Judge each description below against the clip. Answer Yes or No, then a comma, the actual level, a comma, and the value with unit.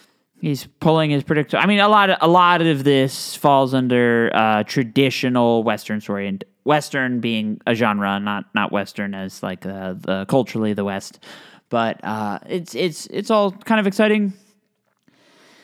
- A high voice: No, low, 135 Hz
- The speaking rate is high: No, average, 165 wpm